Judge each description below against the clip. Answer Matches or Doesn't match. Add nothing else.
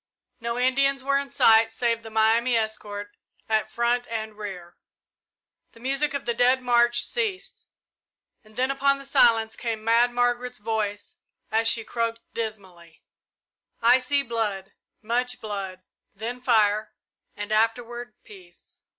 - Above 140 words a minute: Doesn't match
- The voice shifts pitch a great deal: Doesn't match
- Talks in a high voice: Matches